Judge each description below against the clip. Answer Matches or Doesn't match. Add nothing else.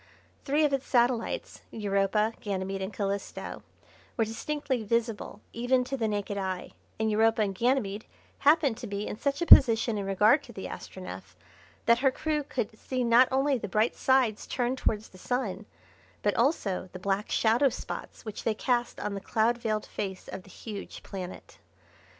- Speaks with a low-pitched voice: Doesn't match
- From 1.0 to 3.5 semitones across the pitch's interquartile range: Doesn't match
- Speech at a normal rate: Matches